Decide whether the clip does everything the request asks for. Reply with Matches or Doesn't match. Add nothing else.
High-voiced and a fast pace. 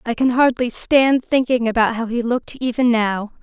Doesn't match